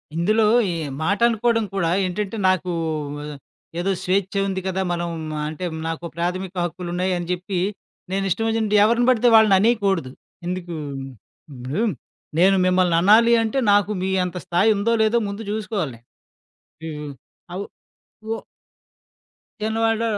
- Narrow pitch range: No, average, 3.7 semitones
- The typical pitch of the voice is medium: No, high, 195 Hz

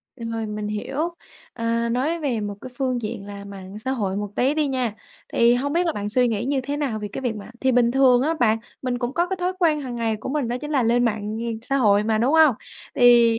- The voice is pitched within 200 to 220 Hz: No, high, 245 Hz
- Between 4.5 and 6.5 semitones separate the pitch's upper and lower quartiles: No, average, 3.7 semitones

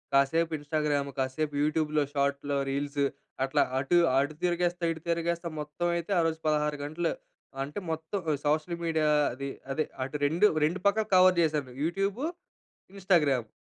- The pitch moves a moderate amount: Yes, average, 3.0 semitones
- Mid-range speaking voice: Yes, medium, 155 Hz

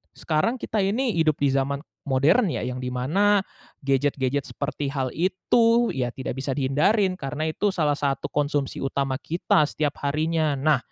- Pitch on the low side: No, medium, 145 Hz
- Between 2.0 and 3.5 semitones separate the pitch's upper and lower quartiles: No, average, 5.0 semitones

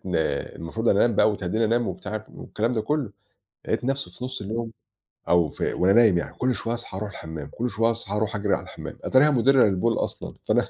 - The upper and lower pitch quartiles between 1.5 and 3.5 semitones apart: Yes, average, 3.2 semitones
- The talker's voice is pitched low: Yes, low, 110 Hz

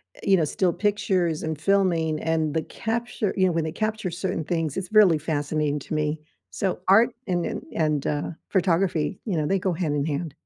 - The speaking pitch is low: No, medium, 170 Hz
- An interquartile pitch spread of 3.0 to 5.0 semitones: Yes, average, 3.7 semitones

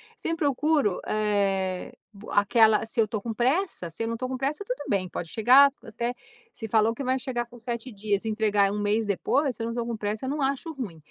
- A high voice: Yes, high, 225 Hz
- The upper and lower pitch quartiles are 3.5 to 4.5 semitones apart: Yes, average, 4.0 semitones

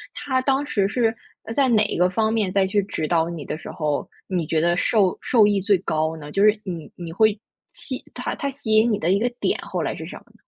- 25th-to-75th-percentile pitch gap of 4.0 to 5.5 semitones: Yes, average, 4.6 semitones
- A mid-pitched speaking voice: No, high, 200 Hz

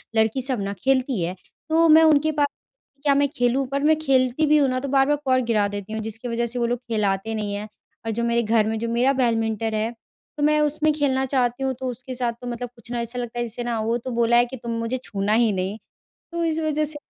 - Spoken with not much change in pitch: No, average, 3.3 semitones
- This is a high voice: Yes, high, 245 Hz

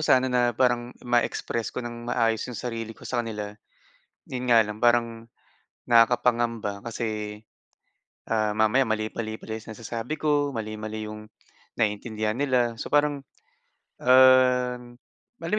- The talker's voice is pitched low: Yes, low, 115 Hz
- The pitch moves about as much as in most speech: No, narrow, 2.3 semitones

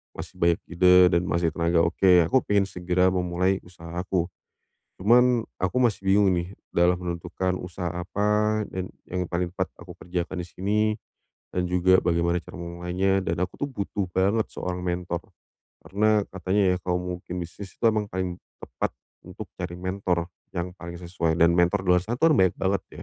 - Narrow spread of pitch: Yes, narrow, 1.8 semitones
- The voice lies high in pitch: No, very low, 90 Hz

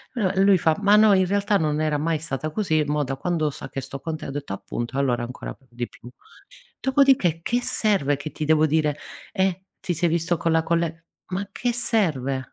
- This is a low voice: No, medium, 160 Hz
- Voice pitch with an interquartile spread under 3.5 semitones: No, average, 4.7 semitones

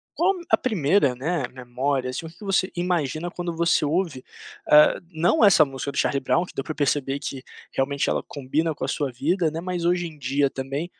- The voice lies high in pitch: No, medium, 150 Hz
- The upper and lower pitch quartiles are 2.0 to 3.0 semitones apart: No, average, 4.3 semitones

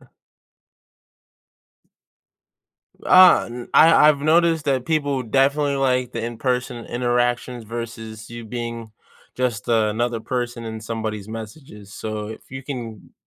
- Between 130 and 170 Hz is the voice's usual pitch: No, low, 120 Hz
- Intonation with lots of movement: No, average, 3.1 semitones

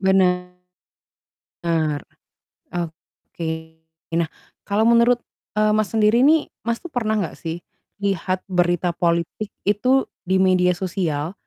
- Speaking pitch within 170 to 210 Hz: Yes, medium, 185 Hz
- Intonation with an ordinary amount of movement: Yes, average, 3.5 semitones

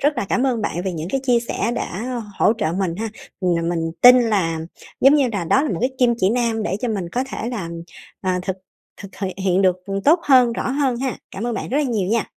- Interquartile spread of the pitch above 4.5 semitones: Yes, average, 5.1 semitones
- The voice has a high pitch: Yes, high, 225 Hz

